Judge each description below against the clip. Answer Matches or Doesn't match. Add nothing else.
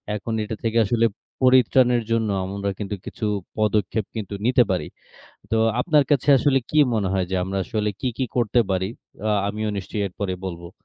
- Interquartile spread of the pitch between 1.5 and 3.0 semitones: Doesn't match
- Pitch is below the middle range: Matches